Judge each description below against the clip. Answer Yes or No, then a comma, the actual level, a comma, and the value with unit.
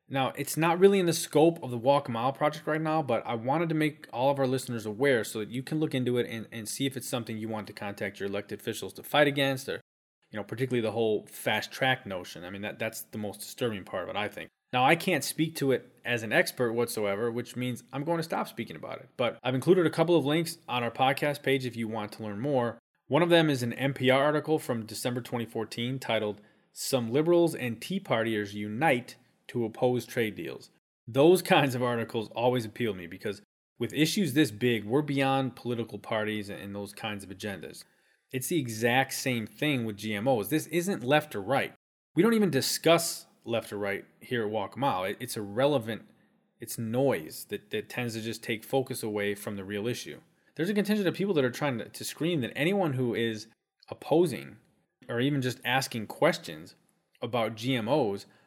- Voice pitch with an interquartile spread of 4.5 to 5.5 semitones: Yes, average, 5.0 semitones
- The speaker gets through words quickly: Yes, fast, 215 wpm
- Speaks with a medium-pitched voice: No, low, 125 Hz